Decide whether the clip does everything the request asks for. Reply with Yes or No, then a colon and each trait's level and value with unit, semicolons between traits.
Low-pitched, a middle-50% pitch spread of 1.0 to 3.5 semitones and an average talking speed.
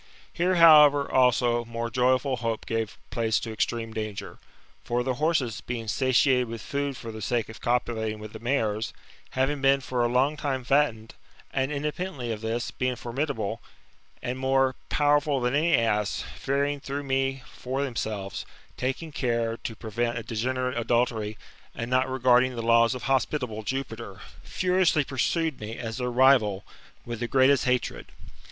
Yes: low, 125 Hz; average, 2.9 semitones; average, 160 wpm